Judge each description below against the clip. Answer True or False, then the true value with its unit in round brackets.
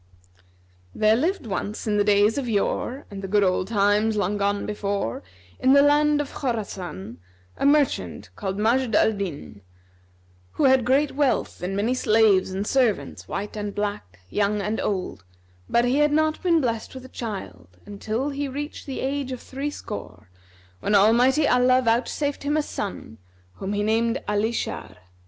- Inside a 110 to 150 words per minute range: False (165 wpm)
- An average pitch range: True (4.7 semitones)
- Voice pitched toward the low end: False (220 Hz)